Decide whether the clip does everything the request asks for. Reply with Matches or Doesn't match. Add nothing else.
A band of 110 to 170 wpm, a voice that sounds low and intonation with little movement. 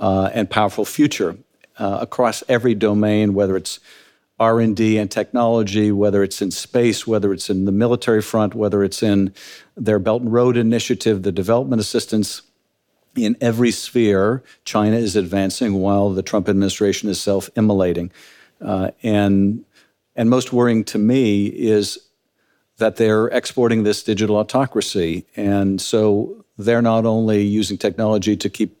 Matches